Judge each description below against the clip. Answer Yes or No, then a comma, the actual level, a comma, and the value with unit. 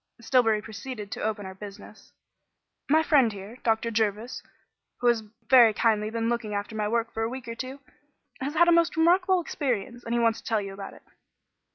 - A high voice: Yes, high, 230 Hz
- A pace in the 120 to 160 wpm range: No, average, 200 wpm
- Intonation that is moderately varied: Yes, average, 3.4 semitones